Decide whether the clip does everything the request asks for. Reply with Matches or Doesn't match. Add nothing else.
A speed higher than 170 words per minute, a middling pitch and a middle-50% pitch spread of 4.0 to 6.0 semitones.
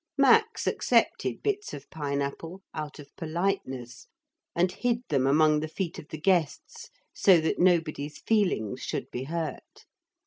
Doesn't match